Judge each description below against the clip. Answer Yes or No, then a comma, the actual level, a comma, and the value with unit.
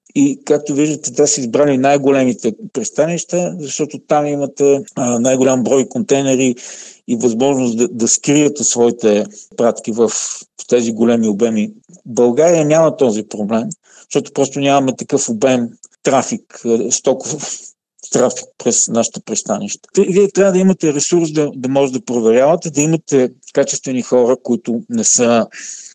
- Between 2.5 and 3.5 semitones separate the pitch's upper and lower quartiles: No, average, 4.1 semitones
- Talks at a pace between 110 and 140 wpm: Yes, average, 135 wpm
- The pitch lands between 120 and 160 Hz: Yes, medium, 140 Hz